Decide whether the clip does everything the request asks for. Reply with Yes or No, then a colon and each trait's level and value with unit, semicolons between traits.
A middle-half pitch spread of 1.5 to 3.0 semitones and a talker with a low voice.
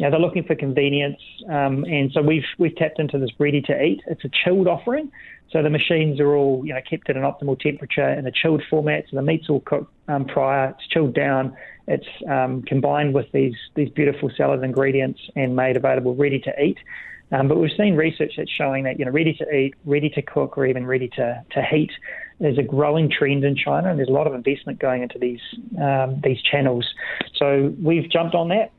No: narrow, 2.5 semitones; medium, 145 Hz